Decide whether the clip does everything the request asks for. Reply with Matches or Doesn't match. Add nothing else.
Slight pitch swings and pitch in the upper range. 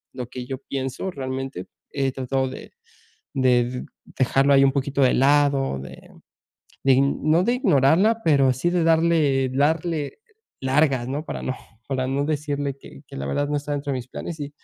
Doesn't match